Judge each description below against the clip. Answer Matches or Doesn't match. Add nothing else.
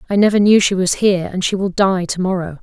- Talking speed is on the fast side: Matches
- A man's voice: Doesn't match